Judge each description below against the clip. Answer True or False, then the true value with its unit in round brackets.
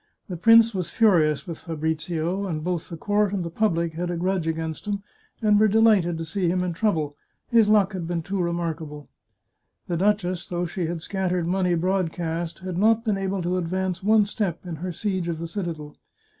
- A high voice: False (180 Hz)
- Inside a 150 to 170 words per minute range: False (200 wpm)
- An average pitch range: True (3.1 semitones)